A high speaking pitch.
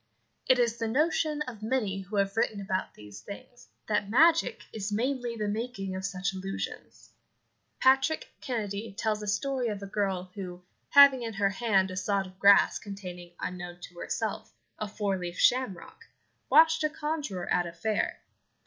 Yes: high, 205 Hz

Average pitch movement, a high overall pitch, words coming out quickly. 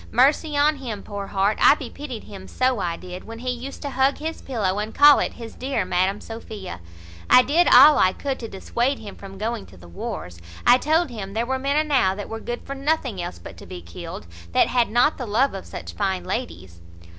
No: wide, 6.0 semitones; high, 230 Hz; fast, 225 wpm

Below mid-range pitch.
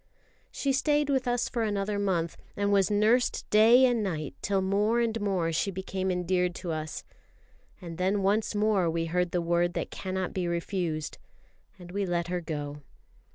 No: high, 190 Hz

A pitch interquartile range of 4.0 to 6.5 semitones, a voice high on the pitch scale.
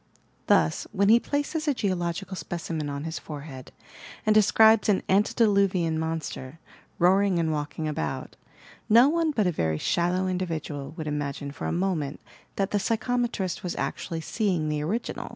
No: average, 5.2 semitones; medium, 180 Hz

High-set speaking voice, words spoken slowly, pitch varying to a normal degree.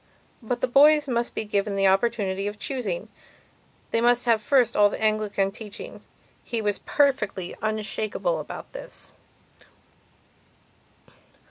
Yes: high, 215 Hz; slow, 130 wpm; average, 3.1 semitones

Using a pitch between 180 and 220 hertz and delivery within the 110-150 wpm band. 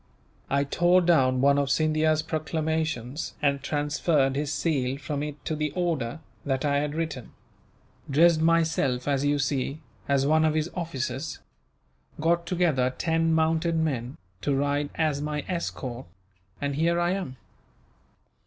No: medium, 150 Hz; average, 145 wpm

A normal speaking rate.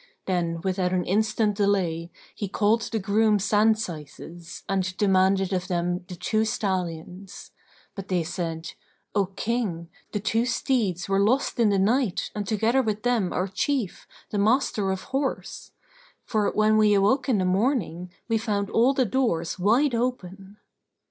Yes: average, 155 wpm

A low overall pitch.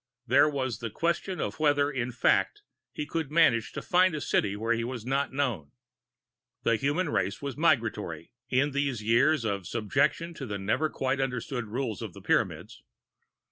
Yes: low, 130 Hz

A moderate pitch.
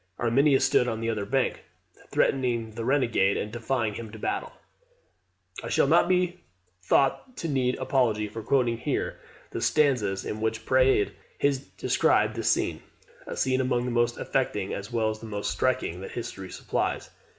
No: low, 120 Hz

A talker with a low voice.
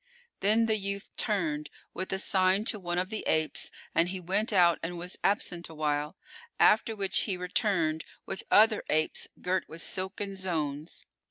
No: medium, 185 Hz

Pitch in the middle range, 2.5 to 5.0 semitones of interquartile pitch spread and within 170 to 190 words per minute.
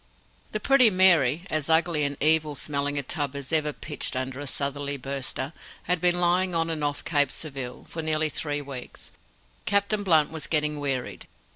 Yes: medium, 150 Hz; average, 2.8 semitones; average, 175 wpm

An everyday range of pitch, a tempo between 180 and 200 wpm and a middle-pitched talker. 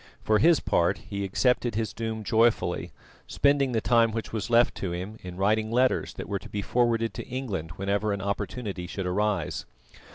No: average, 3.0 semitones; average, 185 wpm; low, 110 Hz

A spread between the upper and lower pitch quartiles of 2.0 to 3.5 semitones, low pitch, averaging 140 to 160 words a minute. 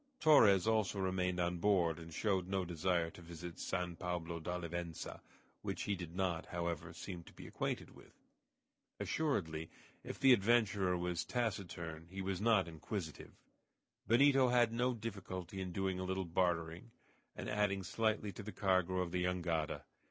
Yes: average, 3.1 semitones; very low, 90 Hz; average, 155 wpm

